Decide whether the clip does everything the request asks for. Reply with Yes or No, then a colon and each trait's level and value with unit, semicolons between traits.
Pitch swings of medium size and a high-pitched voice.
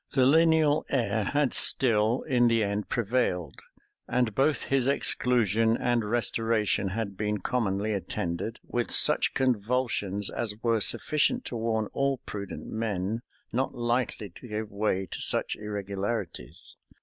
No: average, 3.5 semitones; low, 115 Hz